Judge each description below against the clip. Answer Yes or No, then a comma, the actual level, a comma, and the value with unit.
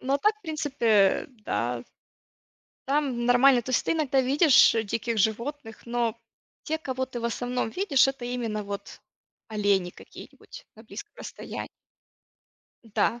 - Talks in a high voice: Yes, high, 245 Hz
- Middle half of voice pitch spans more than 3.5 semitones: Yes, average, 3.9 semitones